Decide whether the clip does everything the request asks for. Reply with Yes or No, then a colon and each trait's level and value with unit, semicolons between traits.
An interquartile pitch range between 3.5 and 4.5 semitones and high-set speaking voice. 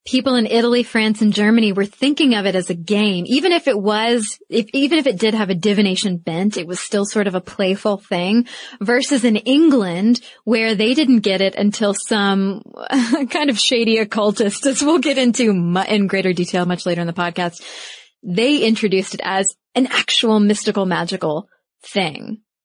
Yes: average, 3.9 semitones; high, 215 Hz